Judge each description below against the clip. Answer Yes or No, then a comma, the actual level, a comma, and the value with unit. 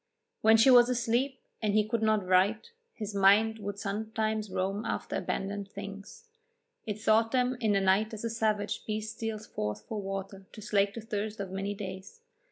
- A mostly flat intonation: Yes, narrow, 1.9 semitones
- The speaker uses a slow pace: No, average, 180 wpm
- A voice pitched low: No, high, 215 Hz